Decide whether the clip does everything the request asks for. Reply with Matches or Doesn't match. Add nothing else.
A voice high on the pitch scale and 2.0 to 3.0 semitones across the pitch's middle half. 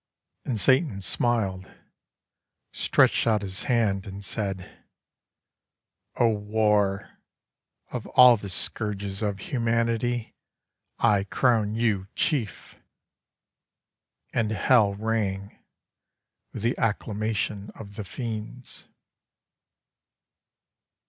Doesn't match